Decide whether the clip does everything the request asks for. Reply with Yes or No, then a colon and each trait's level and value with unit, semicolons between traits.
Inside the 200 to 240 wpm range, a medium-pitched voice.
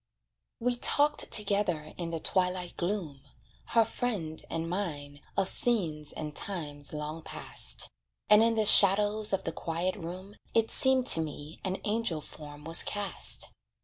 No: average, 145 wpm; medium, 180 Hz